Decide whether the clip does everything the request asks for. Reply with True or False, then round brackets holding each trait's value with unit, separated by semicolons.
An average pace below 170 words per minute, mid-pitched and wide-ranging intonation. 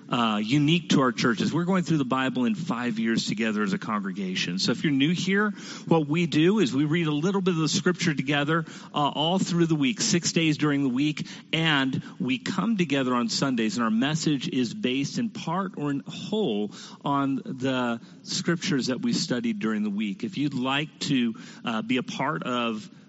False (205 wpm; 160 Hz; 6.0 semitones)